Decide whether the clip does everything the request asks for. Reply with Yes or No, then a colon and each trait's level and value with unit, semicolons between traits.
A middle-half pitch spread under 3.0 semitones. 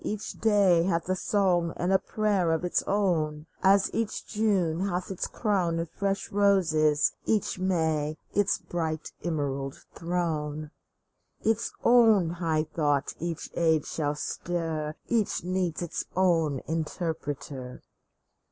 No: average, 3.7 semitones